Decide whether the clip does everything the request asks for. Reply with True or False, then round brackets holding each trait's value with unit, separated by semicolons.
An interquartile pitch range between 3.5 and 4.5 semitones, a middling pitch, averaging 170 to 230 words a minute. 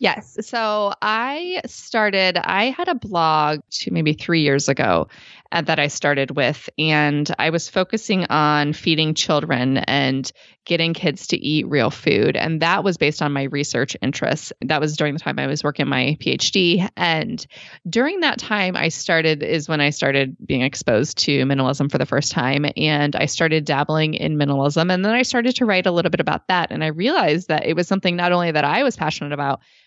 True (4.0 semitones; 155 Hz; 200 wpm)